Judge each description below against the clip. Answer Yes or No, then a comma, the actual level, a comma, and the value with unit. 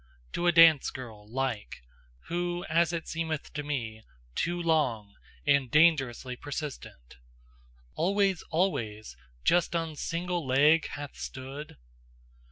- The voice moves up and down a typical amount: Yes, average, 4.7 semitones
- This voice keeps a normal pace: No, slow, 115 wpm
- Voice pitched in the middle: Yes, medium, 150 Hz